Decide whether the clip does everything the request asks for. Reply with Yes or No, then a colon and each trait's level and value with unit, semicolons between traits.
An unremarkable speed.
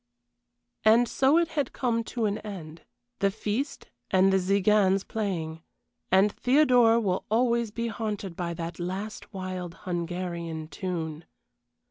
No: slow, 130 wpm